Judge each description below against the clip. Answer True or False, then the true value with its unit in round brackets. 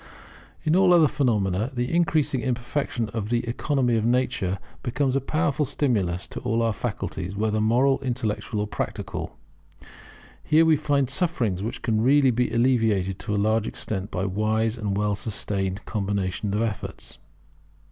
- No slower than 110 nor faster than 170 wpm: True (155 wpm)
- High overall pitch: False (115 Hz)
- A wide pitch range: False (4.3 semitones)